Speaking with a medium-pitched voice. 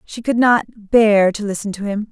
No: high, 215 Hz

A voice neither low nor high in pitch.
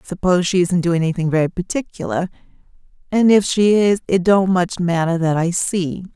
Yes: medium, 180 Hz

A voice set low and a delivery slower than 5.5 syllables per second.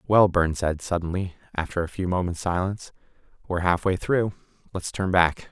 No: very low, 90 Hz; 5.6 syllables/s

